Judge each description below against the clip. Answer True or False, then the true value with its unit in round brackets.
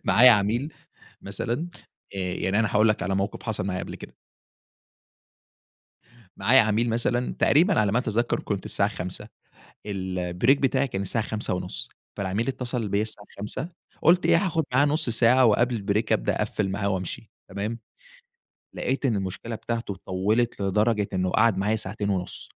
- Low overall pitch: True (105 Hz)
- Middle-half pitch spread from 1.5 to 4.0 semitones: True (3.6 semitones)